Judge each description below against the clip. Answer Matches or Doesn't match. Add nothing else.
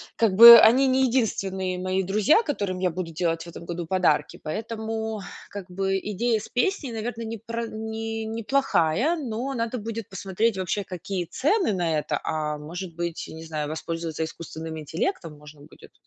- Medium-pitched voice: Doesn't match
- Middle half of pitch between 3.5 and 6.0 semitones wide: Matches